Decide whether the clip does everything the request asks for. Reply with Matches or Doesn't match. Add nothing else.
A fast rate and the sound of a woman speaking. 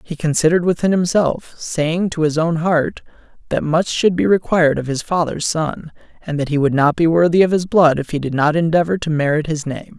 Doesn't match